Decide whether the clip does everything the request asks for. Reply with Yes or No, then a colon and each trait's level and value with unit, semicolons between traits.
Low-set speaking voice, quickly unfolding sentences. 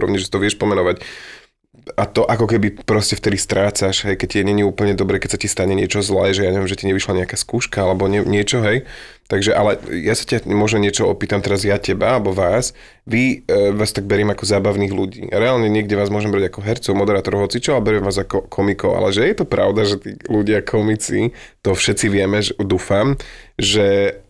Yes: low, 100 Hz; fast, 210 wpm